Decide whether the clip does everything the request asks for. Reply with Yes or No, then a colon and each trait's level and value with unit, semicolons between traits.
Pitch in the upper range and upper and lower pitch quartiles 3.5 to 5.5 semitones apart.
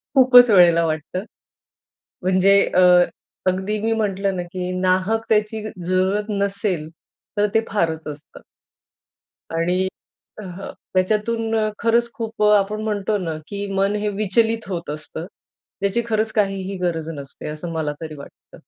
No: high, 195 Hz; average, 3.1 semitones